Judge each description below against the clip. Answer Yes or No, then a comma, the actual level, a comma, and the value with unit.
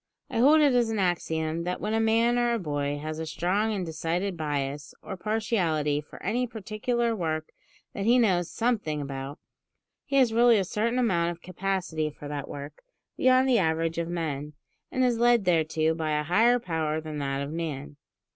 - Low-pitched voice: No, medium, 175 Hz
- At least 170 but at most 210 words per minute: Yes, average, 190 wpm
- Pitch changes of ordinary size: No, wide, 6.4 semitones